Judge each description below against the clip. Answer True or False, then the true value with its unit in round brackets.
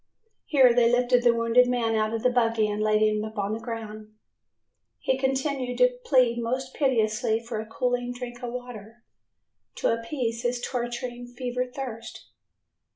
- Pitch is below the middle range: False (240 Hz)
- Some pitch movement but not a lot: False (1.8 semitones)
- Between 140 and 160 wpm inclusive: True (155 wpm)